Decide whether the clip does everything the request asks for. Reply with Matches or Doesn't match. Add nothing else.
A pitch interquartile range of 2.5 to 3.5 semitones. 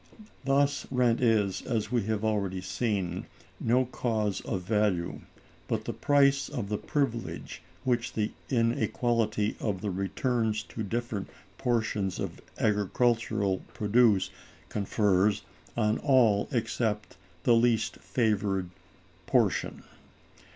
Matches